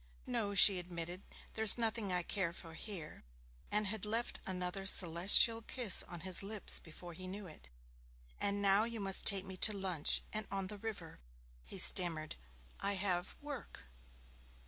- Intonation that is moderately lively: Yes, average, 3.1 semitones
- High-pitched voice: Yes, high, 195 Hz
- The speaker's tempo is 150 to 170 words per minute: Yes, average, 160 wpm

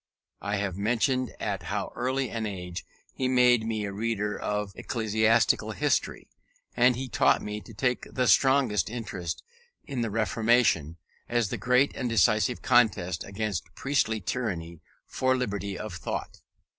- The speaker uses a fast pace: No, average, 145 wpm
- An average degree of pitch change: Yes, average, 3.7 semitones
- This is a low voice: Yes, low, 110 Hz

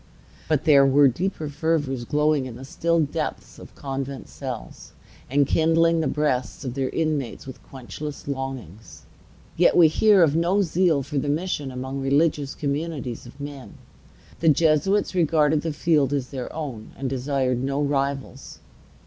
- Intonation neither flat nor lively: Yes, average, 3.0 semitones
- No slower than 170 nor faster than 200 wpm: No, average, 155 wpm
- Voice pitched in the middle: Yes, medium, 145 Hz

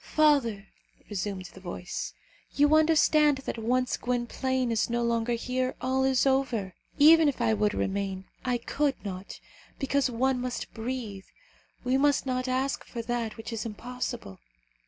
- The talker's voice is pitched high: Yes, high, 245 Hz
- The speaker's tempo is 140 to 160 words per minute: Yes, average, 150 wpm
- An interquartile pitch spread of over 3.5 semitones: No, average, 3.1 semitones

